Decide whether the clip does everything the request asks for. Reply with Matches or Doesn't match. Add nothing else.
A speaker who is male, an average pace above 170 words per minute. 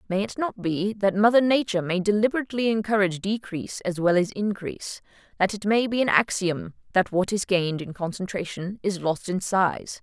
Doesn't match